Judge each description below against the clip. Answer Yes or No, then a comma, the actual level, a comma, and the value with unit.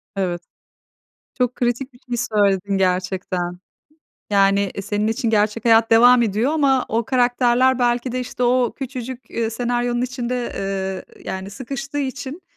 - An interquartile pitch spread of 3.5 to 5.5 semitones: Yes, average, 4.0 semitones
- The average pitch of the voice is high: Yes, high, 240 Hz